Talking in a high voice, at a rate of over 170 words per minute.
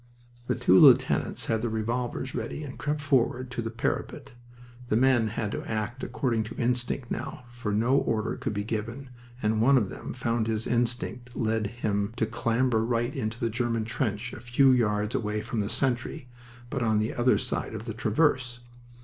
No: low, 115 Hz; average, 185 wpm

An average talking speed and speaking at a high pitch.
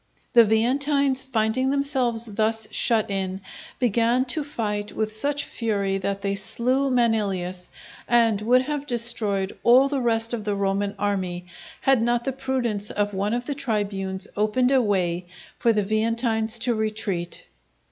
Yes: average, 150 wpm; high, 225 Hz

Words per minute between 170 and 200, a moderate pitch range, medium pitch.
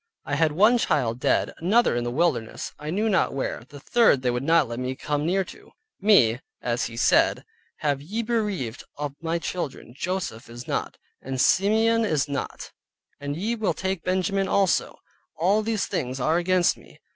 No: average, 180 wpm; wide, 6.8 semitones; medium, 165 Hz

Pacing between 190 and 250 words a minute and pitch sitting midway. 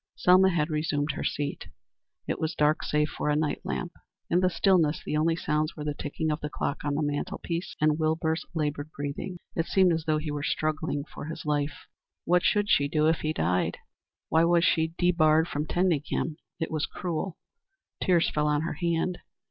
Yes: average, 200 wpm; medium, 155 Hz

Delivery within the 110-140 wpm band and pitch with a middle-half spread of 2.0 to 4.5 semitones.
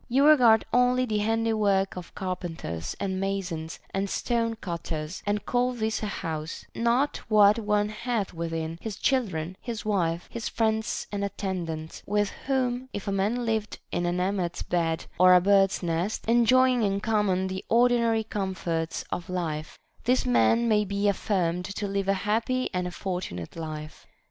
No: average, 160 wpm; average, 4.1 semitones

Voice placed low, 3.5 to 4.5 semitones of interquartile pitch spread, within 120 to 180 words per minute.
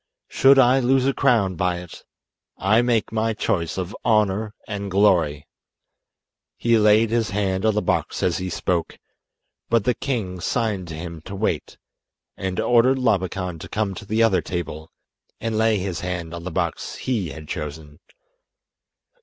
Yes: low, 100 Hz; average, 4.2 semitones; average, 160 wpm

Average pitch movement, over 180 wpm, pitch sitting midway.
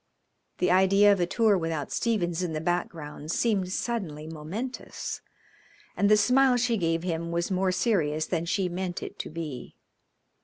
No: average, 3.9 semitones; average, 160 wpm; medium, 180 Hz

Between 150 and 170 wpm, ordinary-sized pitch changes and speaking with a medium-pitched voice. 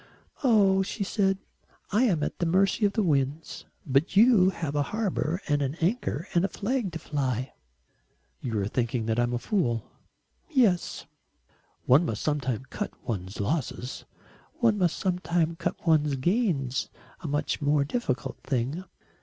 No: average, 155 wpm; wide, 6.5 semitones; medium, 160 Hz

